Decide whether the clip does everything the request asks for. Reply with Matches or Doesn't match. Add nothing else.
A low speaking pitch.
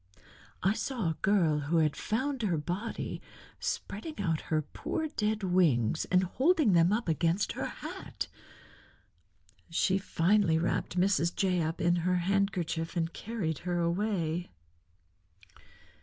Doesn't match